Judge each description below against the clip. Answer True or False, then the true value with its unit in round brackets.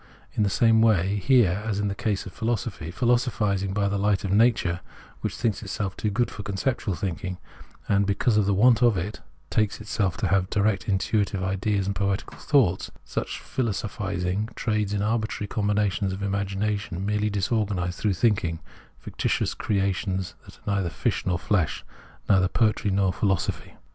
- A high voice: False (100 Hz)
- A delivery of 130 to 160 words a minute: False (175 wpm)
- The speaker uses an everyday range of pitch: False (2.0 semitones)